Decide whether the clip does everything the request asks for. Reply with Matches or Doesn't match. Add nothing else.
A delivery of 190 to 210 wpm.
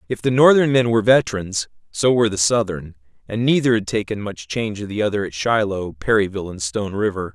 Matches